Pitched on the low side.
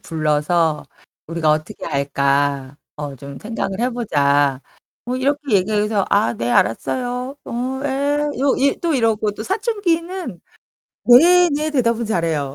No: high, 215 Hz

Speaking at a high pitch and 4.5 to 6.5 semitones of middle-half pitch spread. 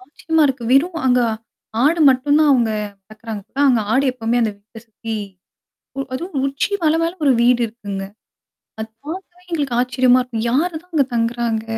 Yes: very high, 255 Hz; average, 4.8 semitones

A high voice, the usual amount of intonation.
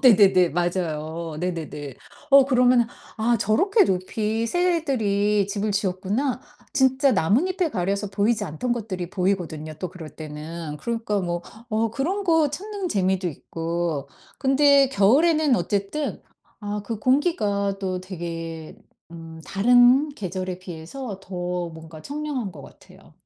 No: high, 200 Hz; wide, 6.7 semitones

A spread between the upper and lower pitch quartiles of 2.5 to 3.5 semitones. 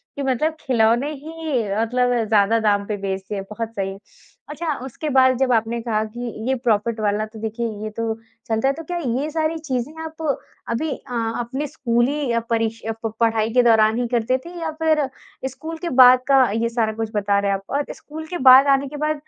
No: average, 4.4 semitones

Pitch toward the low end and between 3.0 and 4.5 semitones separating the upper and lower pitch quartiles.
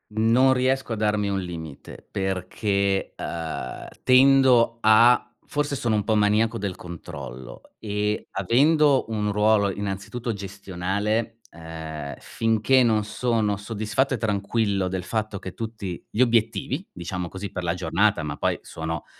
Yes: low, 105 Hz; average, 3.5 semitones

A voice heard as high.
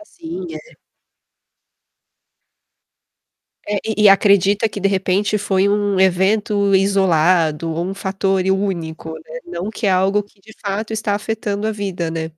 Yes: high, 195 Hz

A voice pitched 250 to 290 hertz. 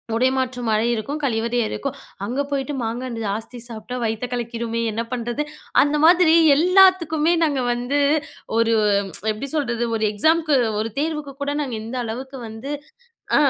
Yes: very high, 255 Hz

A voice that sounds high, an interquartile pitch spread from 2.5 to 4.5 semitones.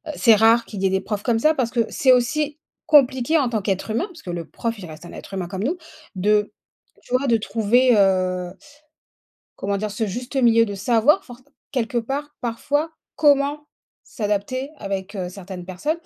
No: high, 230 Hz; average, 4.9 semitones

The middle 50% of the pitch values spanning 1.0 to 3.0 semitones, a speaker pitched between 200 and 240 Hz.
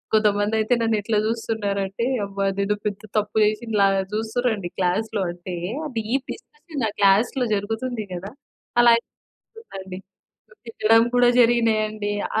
Yes: narrow, 2.5 semitones; high, 215 Hz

